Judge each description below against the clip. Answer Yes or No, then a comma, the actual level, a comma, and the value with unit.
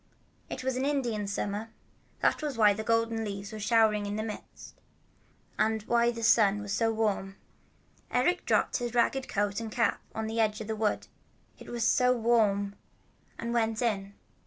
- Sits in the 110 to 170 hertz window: No, high, 220 Hz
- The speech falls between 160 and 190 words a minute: Yes, average, 175 wpm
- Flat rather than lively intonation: Yes, narrow, 2.2 semitones